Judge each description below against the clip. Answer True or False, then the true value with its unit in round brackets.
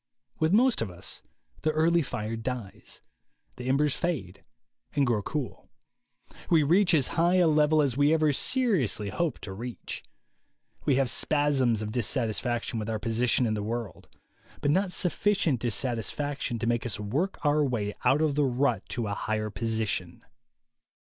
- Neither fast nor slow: True (160 wpm)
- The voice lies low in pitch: True (125 Hz)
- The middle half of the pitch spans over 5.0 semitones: True (5.4 semitones)